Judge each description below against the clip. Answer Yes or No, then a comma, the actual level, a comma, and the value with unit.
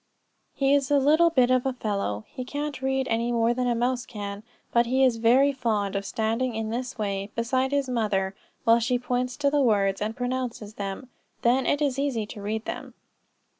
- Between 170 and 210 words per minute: Yes, fast, 205 wpm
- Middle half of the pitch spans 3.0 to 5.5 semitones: Yes, average, 3.3 semitones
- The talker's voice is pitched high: Yes, high, 245 Hz